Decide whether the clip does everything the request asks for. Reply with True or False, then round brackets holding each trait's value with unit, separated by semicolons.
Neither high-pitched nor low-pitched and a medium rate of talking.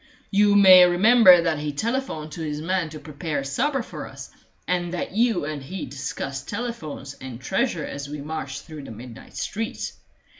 True (160 Hz; 175 wpm)